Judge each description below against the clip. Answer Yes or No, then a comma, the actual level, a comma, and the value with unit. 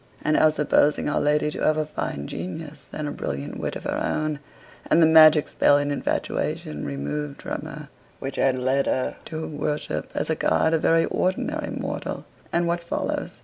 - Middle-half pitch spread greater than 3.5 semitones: No, average, 3.2 semitones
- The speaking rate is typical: Yes, average, 190 wpm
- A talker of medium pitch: Yes, medium, 150 Hz